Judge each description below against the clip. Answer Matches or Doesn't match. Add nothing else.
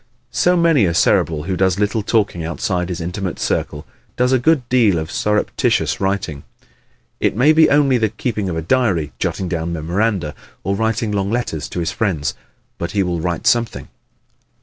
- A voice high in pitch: Doesn't match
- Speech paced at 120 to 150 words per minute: Doesn't match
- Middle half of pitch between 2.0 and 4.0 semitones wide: Doesn't match